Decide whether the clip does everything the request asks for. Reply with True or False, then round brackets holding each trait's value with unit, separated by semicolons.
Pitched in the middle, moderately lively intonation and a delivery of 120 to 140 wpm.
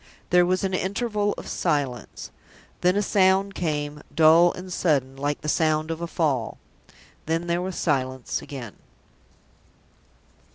True (165 Hz; 4.0 semitones; 135 wpm)